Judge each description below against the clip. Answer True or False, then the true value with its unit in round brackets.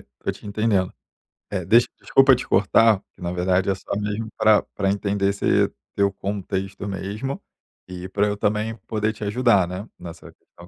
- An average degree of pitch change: False (2.1 semitones)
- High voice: False (100 Hz)